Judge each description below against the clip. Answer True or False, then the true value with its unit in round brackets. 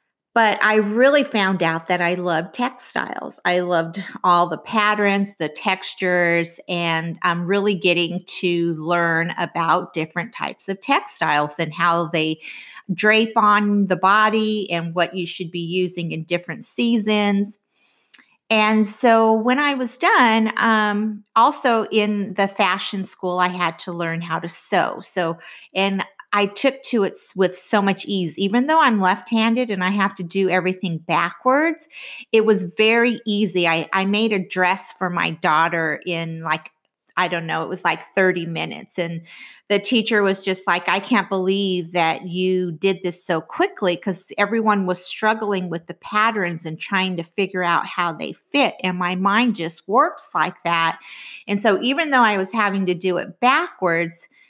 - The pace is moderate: True (170 wpm)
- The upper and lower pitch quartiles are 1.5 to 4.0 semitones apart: True (3.7 semitones)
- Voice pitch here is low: False (190 Hz)